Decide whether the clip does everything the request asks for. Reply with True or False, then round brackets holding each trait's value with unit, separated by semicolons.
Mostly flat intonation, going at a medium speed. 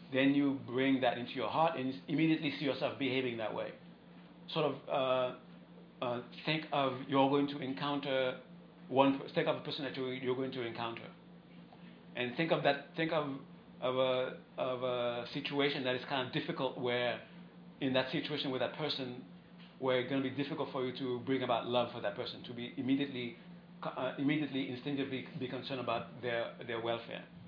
True (2.3 semitones; 190 wpm)